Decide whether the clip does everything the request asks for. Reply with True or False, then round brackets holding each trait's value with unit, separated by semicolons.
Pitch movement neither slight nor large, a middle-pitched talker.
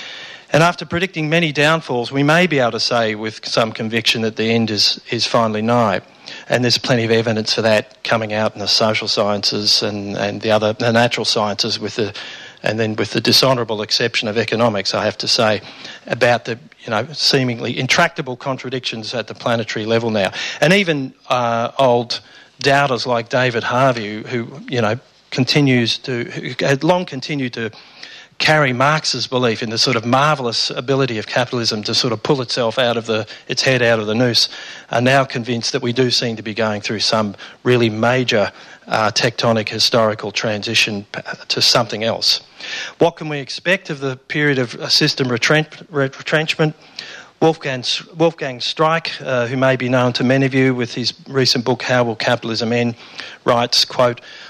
False (3.1 semitones; 120 Hz)